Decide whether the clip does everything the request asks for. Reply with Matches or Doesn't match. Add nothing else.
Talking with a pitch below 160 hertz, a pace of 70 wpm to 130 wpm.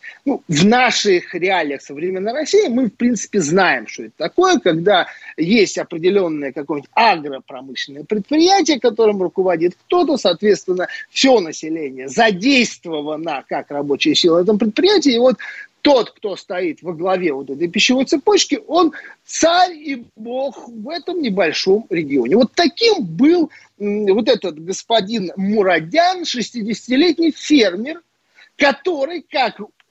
Doesn't match